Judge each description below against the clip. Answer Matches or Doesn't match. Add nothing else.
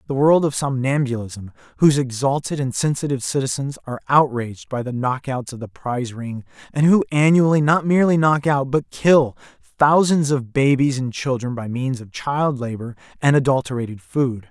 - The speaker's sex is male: Matches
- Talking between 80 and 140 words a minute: Doesn't match